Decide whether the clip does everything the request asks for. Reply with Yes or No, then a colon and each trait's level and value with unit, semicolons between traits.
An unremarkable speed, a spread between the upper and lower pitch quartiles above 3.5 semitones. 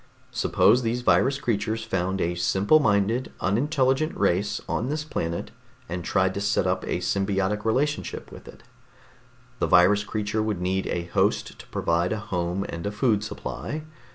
Yes: average, 160 wpm; average, 3.9 semitones